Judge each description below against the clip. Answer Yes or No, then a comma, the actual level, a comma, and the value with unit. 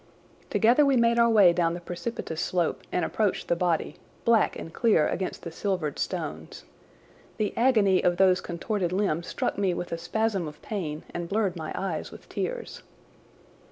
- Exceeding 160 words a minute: Yes, average, 170 wpm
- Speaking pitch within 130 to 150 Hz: No, medium, 185 Hz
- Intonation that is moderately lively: Yes, average, 4.3 semitones